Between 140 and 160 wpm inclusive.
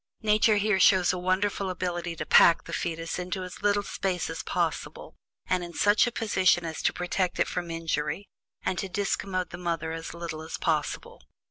No: average, 190 wpm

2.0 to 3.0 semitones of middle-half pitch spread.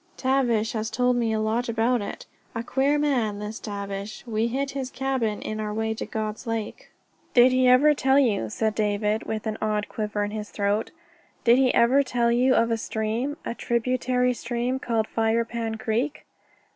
Yes: narrow, 2.6 semitones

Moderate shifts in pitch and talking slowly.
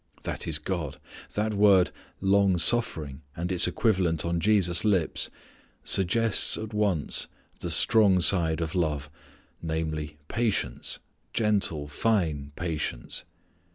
Yes: average, 4.5 semitones; slow, 115 wpm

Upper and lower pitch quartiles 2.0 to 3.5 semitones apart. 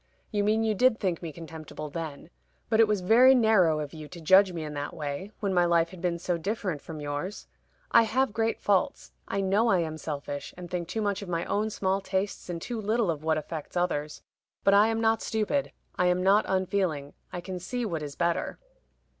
No: average, 4.5 semitones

